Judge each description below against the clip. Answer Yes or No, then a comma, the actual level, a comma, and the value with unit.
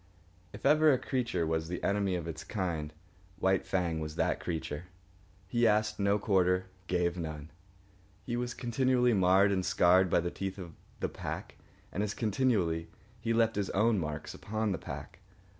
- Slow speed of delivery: No, average, 170 wpm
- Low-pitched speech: Yes, very low, 95 Hz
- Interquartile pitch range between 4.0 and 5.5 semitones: Yes, average, 4.3 semitones